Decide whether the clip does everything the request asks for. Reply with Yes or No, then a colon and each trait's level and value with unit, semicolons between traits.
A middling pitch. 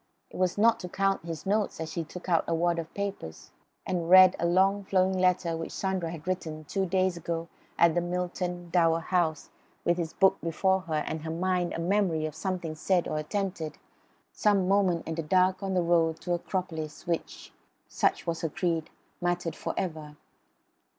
Yes: medium, 175 Hz